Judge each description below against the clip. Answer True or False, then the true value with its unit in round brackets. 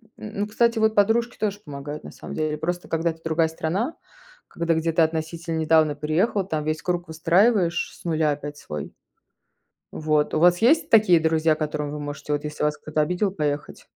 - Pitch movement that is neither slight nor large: True (3.1 semitones)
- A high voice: False (160 Hz)